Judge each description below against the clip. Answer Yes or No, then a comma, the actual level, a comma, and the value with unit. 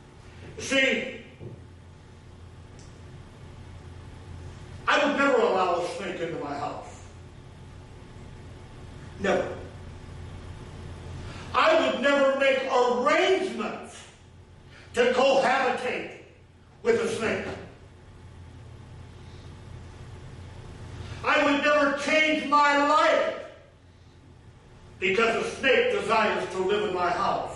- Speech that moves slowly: Yes, slow, 80 wpm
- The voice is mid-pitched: Yes, medium, 175 Hz